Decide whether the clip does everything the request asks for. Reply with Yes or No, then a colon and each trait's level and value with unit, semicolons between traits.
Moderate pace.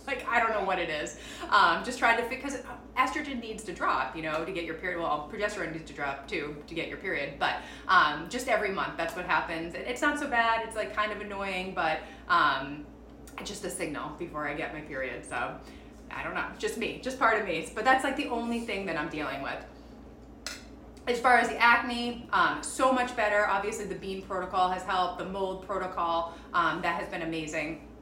No: fast, 220 wpm